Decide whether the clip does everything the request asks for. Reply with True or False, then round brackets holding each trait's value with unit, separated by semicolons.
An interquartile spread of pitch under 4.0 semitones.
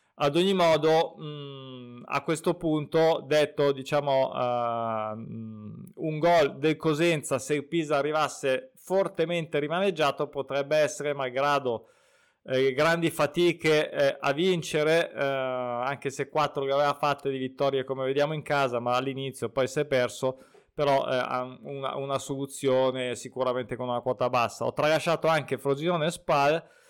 True (3.0 semitones)